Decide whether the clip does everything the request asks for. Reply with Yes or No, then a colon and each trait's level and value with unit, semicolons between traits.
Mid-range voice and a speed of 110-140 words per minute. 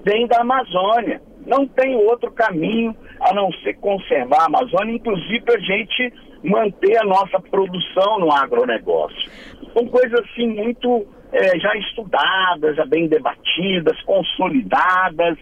No: high, 225 Hz; average, 130 wpm